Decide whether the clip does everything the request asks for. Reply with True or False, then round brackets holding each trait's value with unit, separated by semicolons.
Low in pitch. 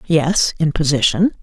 False (160 Hz)